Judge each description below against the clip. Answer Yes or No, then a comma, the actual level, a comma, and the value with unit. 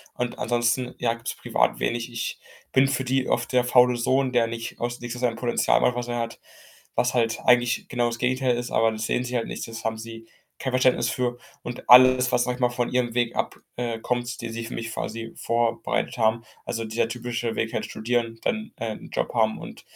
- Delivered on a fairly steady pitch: Yes, narrow, 1.3 semitones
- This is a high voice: No, low, 120 Hz